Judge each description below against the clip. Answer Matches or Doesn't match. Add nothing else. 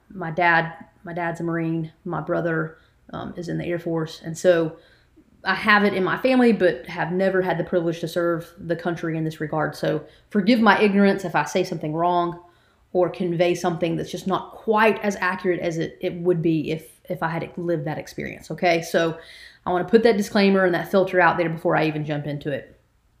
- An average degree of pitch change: Doesn't match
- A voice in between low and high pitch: Matches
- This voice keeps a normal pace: Doesn't match